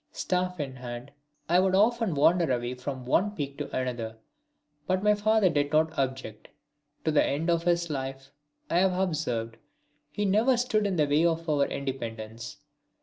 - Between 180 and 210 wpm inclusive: No, average, 170 wpm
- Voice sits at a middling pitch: Yes, medium, 155 Hz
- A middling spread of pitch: No, wide, 5.8 semitones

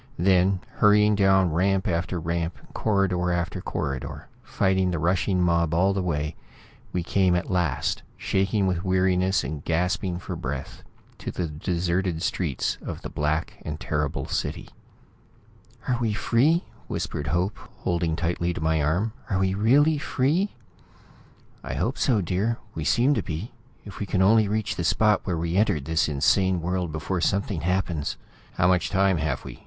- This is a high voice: No, very low, 90 Hz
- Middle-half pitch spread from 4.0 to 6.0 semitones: No, average, 2.9 semitones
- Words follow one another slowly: No, average, 165 wpm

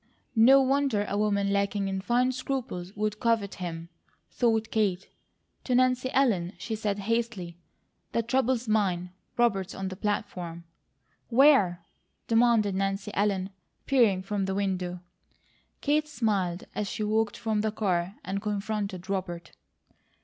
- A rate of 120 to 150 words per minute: Yes, slow, 135 wpm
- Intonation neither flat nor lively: Yes, average, 3.4 semitones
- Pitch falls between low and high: No, high, 205 Hz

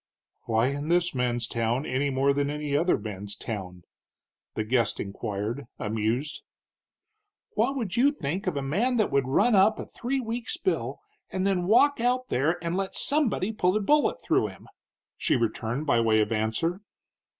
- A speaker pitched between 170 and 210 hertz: No, medium, 145 Hz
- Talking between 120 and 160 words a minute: No, average, 170 wpm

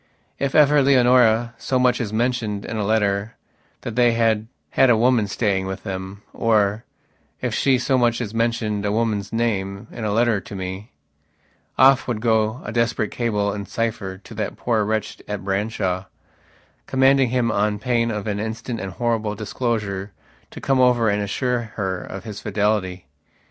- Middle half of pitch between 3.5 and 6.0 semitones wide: No, average, 2.8 semitones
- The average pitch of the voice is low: Yes, low, 110 Hz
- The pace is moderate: Yes, average, 165 wpm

